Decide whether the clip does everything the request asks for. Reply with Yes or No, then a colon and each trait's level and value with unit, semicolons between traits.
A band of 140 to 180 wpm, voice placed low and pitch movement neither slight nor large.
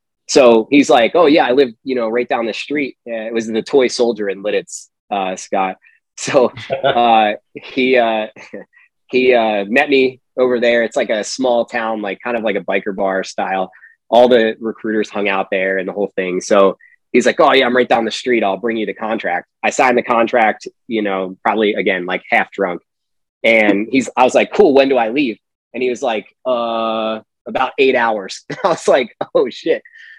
No: fast, 205 wpm; low, 115 Hz; average, 3.7 semitones